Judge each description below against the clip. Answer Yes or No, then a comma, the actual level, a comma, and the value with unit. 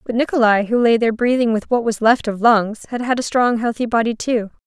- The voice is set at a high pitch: Yes, high, 230 Hz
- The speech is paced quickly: Yes, fast, 245 wpm